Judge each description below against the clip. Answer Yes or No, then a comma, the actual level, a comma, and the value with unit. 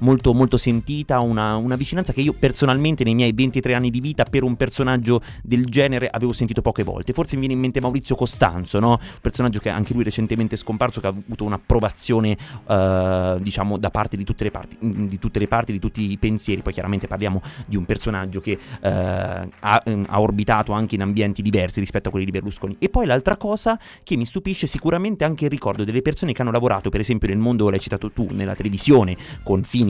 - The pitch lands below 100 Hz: No, low, 115 Hz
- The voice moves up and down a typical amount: Yes, average, 3.9 semitones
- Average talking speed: No, fast, 215 wpm